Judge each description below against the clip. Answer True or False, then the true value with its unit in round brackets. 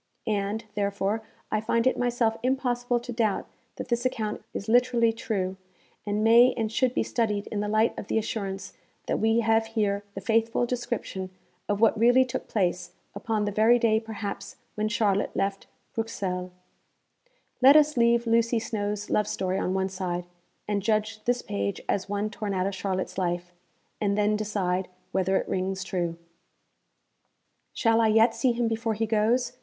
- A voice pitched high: True (215 Hz)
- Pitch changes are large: False (2.7 semitones)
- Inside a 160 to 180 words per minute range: True (170 wpm)